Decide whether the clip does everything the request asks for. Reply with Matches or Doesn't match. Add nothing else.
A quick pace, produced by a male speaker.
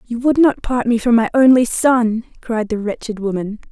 Doesn't match